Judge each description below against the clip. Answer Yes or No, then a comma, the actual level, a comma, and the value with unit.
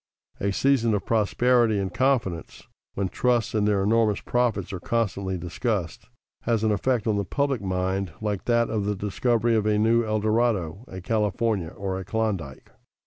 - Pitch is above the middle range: No, low, 105 Hz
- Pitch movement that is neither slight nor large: Yes, average, 3.2 semitones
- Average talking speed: Yes, average, 170 wpm